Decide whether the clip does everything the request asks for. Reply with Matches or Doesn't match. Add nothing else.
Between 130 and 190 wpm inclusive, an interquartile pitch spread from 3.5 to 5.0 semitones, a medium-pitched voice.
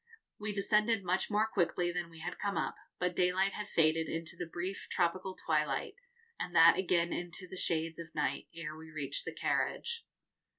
Doesn't match